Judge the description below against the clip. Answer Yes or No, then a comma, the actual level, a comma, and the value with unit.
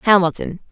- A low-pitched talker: No, medium, 185 Hz